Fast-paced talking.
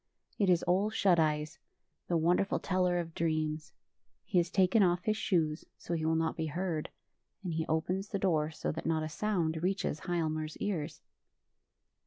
No: average, 175 wpm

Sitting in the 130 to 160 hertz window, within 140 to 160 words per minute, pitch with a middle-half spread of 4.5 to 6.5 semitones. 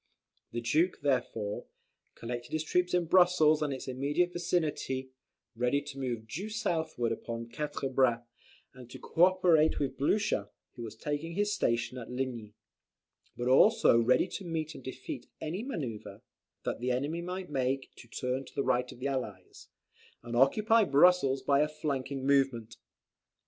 Yes: low, 135 Hz; average, 155 wpm; average, 5.1 semitones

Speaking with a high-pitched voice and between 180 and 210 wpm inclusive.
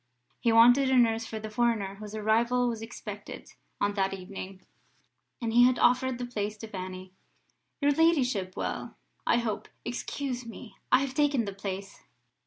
No: high, 225 Hz; average, 165 wpm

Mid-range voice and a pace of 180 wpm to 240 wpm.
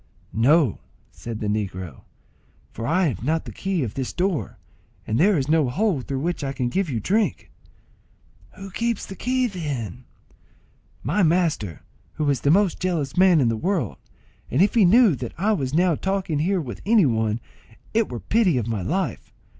Yes: medium, 160 Hz; average, 185 wpm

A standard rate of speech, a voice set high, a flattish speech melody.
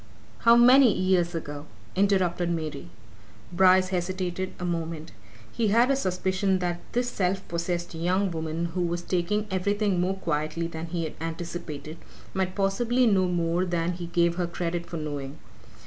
No: average, 155 wpm; medium, 175 Hz; narrow, 2.2 semitones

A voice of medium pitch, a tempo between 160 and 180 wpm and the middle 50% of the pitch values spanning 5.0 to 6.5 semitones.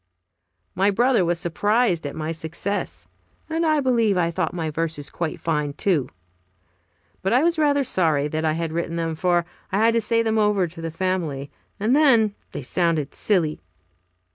Yes: medium, 175 Hz; average, 175 wpm; wide, 5.5 semitones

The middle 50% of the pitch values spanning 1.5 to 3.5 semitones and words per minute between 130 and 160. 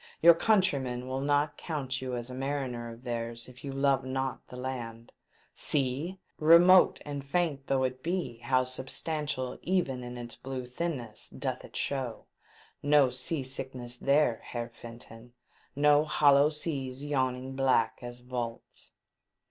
Yes: average, 2.9 semitones; average, 150 wpm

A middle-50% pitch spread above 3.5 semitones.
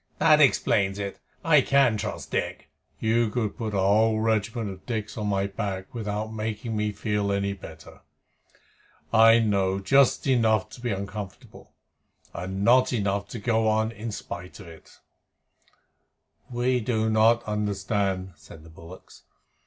No: narrow, 2.4 semitones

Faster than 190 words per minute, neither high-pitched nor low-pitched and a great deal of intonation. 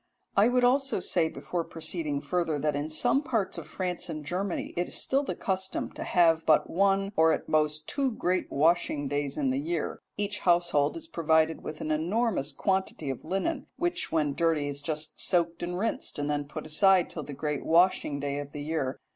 No: average, 200 wpm; medium, 165 Hz; average, 4.2 semitones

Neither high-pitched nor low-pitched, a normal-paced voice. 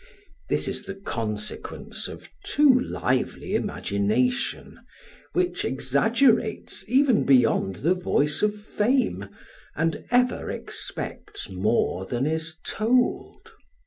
No: medium, 180 Hz; slow, 100 wpm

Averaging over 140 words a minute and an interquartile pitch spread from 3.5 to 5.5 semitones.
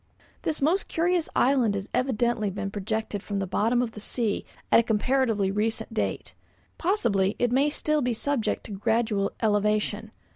Yes: average, 160 wpm; average, 3.9 semitones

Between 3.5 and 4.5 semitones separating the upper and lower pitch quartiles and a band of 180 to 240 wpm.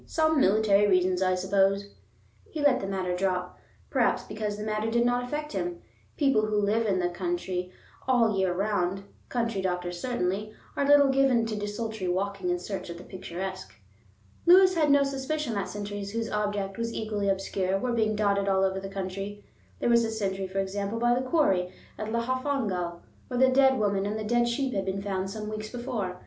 Yes: average, 3.8 semitones; average, 195 wpm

